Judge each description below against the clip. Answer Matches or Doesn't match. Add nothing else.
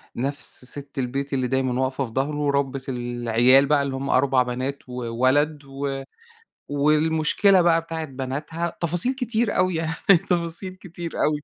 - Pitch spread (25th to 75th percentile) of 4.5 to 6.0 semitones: Doesn't match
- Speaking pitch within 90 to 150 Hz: Matches